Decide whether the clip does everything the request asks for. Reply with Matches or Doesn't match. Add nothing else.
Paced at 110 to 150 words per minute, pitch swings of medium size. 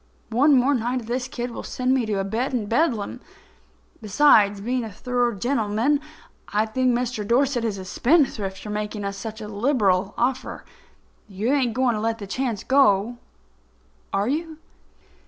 Doesn't match